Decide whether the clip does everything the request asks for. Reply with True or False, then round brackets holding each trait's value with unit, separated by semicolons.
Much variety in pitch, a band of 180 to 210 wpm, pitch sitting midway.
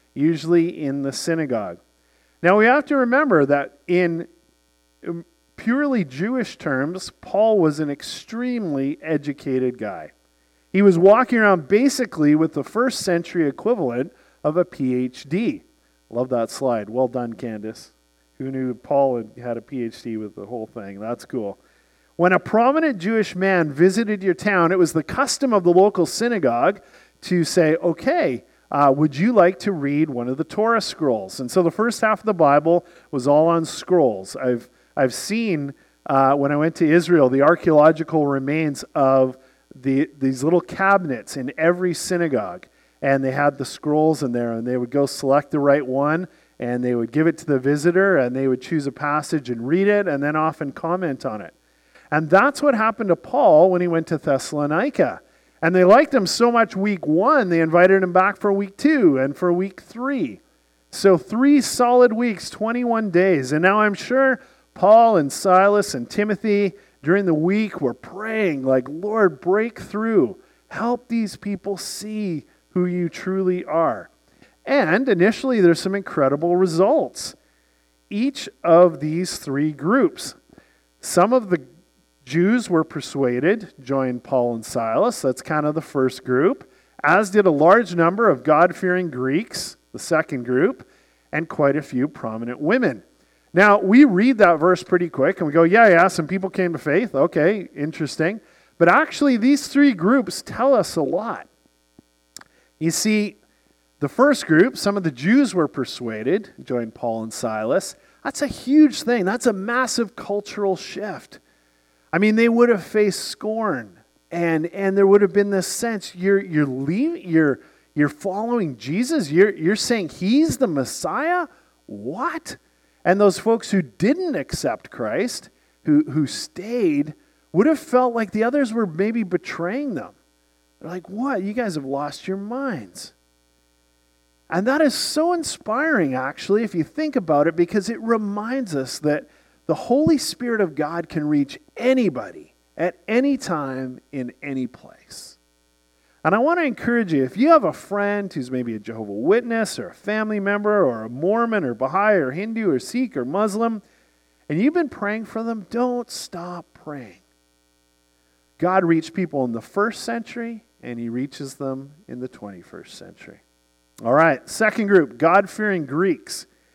False (7.8 semitones; 165 wpm; 175 Hz)